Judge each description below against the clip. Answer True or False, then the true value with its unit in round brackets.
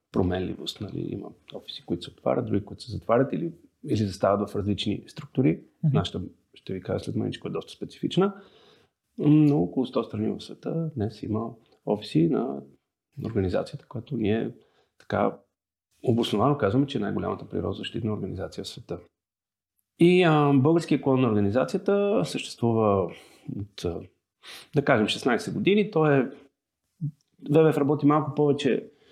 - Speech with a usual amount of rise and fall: False (6.8 semitones)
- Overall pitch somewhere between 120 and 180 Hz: True (135 Hz)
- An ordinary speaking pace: True (135 wpm)